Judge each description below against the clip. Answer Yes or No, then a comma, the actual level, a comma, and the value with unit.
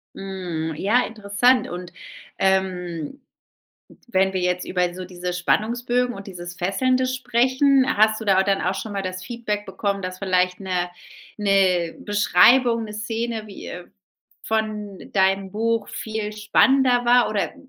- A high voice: Yes, high, 205 Hz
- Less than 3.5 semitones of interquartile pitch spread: No, average, 3.9 semitones